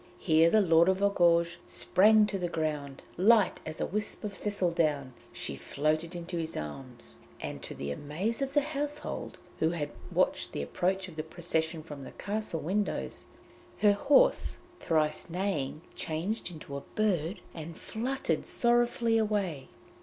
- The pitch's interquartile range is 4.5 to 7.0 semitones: Yes, average, 5.1 semitones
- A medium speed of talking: Yes, average, 155 wpm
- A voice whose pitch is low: No, medium, 175 Hz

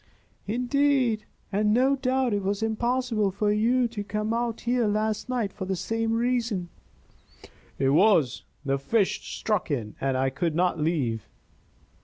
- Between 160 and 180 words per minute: No, average, 150 wpm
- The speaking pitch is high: Yes, high, 215 Hz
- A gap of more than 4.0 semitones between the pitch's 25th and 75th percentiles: Yes, average, 5.0 semitones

